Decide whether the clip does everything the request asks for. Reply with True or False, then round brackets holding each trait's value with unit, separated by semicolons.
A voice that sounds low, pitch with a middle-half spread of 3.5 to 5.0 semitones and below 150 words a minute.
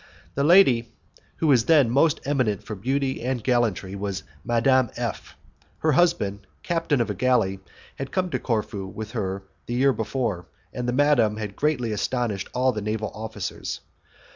False (120 Hz; 4.4 semitones; 160 wpm)